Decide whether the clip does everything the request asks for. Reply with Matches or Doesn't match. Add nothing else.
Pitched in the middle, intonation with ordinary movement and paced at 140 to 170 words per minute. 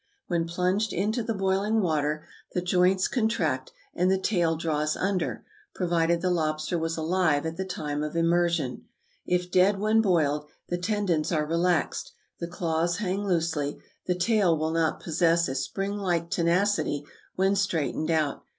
Matches